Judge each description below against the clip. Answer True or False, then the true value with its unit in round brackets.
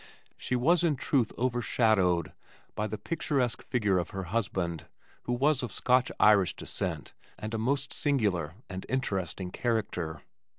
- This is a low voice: True (110 Hz)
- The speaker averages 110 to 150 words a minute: True (140 wpm)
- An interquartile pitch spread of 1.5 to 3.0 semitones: False (5.3 semitones)